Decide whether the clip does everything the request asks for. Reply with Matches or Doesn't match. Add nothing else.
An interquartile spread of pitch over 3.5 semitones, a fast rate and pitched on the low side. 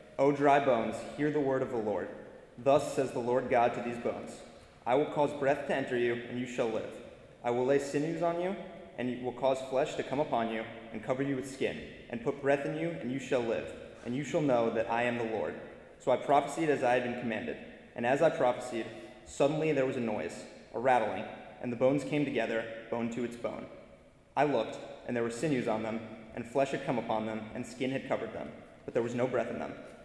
Doesn't match